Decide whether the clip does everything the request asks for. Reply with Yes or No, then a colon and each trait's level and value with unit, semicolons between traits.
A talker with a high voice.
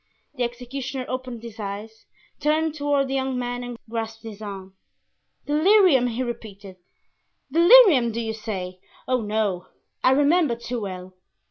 Yes: high, 240 Hz